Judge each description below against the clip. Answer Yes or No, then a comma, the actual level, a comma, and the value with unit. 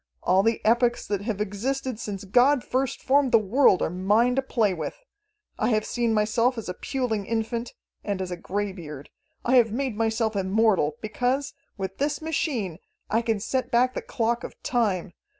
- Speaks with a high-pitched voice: Yes, high, 225 Hz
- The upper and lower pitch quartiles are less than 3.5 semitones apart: No, average, 3.8 semitones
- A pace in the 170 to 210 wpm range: Yes, average, 180 wpm